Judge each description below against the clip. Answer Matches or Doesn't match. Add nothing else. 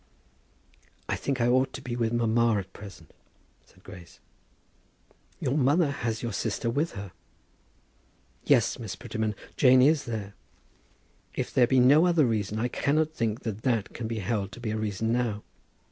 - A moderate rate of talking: Matches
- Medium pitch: Doesn't match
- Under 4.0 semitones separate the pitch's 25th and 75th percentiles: Matches